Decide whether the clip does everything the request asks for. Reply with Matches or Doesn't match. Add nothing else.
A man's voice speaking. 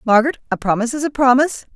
Doesn't match